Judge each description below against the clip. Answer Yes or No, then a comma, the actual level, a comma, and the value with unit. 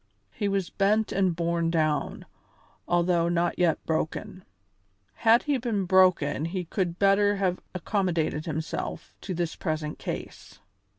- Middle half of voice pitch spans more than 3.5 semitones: No, average, 2.9 semitones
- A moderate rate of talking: No, slow, 130 wpm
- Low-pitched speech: No, medium, 180 Hz